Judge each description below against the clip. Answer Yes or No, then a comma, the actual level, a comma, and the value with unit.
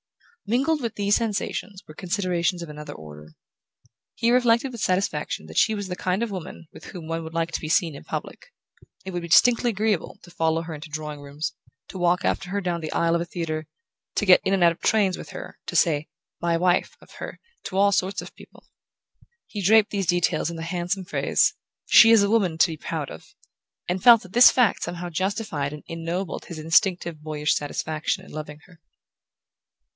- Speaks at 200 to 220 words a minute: Yes, fast, 205 wpm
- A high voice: No, medium, 175 Hz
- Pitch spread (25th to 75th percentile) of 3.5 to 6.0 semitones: Yes, average, 3.9 semitones